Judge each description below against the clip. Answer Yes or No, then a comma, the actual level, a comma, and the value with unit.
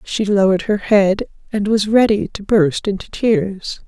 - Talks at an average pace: Yes, average, 170 wpm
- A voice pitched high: Yes, high, 200 Hz